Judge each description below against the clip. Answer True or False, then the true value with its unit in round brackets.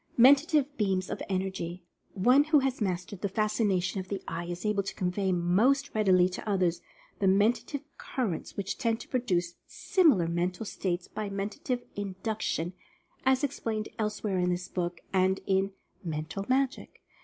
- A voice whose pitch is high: True (195 Hz)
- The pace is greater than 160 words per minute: False (155 wpm)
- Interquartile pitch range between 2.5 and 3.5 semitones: False (4.2 semitones)